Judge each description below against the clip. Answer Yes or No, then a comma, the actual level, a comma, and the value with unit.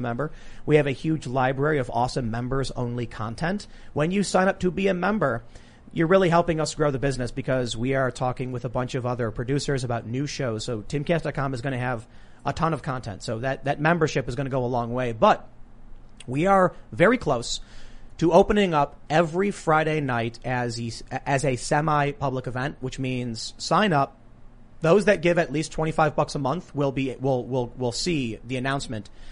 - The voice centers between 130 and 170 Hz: Yes, low, 135 Hz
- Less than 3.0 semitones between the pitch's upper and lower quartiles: No, average, 4.0 semitones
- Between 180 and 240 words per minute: Yes, average, 200 wpm